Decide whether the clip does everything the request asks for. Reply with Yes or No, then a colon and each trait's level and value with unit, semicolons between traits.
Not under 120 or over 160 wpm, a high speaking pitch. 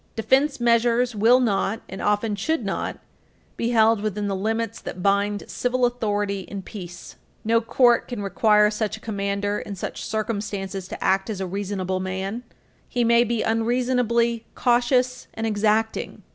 Yes: average, 155 wpm; high, 220 Hz